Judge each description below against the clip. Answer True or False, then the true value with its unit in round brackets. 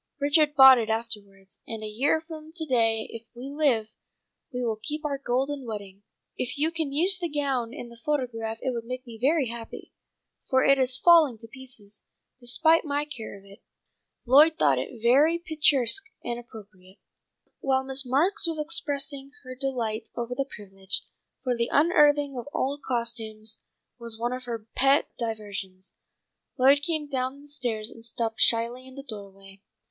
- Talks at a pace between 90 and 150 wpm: False (170 wpm)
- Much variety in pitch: False (4.3 semitones)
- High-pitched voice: True (255 Hz)